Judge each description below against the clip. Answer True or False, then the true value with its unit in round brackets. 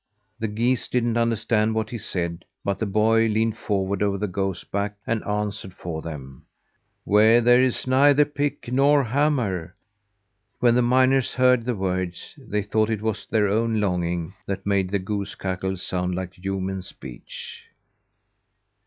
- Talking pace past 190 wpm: False (155 wpm)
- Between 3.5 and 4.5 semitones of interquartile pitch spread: True (3.8 semitones)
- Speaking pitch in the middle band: False (105 Hz)